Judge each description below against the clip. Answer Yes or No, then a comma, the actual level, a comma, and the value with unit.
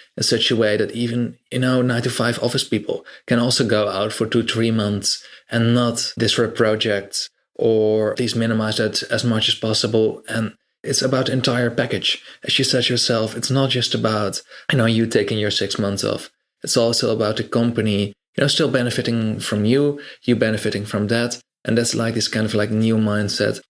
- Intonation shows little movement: Yes, narrow, 2.2 semitones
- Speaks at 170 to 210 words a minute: Yes, average, 200 wpm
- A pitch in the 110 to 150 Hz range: Yes, low, 115 Hz